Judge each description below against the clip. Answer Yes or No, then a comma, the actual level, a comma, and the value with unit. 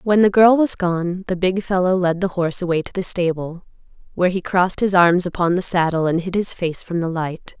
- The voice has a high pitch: No, medium, 180 Hz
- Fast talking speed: Yes, fast, 235 wpm